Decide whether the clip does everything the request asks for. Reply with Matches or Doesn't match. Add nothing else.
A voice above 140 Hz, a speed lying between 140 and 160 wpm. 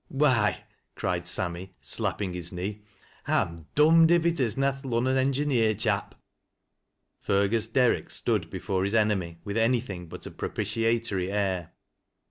Doesn't match